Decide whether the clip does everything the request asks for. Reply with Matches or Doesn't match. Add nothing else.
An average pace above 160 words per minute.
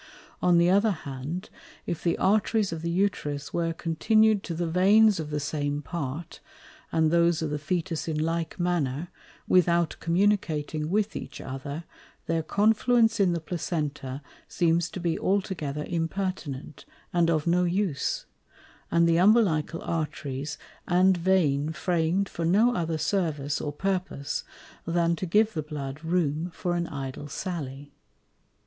Doesn't match